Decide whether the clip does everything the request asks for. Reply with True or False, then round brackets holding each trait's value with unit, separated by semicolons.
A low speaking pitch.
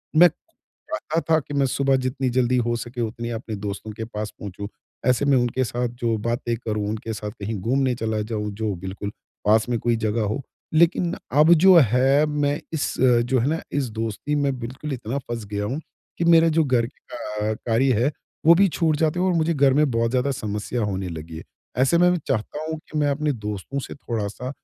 True (125 Hz)